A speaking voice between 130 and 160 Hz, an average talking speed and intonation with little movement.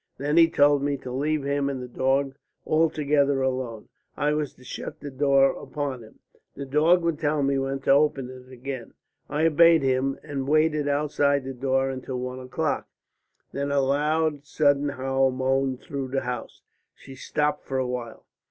Yes: medium, 140 Hz; average, 180 wpm; narrow, 2.0 semitones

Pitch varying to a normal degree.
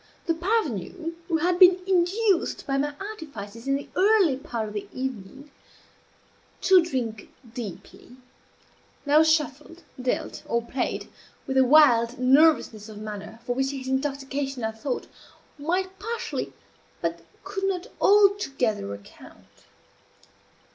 No: wide, 6.8 semitones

